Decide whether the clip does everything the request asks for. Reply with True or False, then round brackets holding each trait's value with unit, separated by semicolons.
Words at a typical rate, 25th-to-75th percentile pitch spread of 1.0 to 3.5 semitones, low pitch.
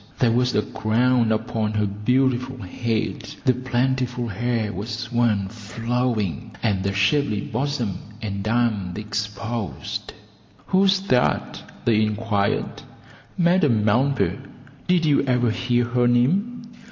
False (115 wpm; 3.1 semitones; 120 Hz)